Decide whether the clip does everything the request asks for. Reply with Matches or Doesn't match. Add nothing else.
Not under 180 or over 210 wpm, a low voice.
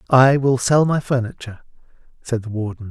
Doesn't match